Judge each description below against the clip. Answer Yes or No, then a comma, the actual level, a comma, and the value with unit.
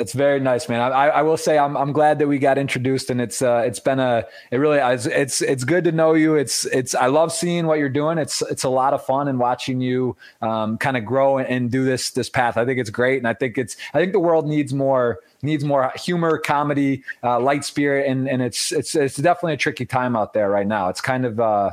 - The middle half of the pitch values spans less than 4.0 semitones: Yes, average, 2.8 semitones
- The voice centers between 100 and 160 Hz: Yes, low, 135 Hz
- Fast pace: Yes, fast, 260 wpm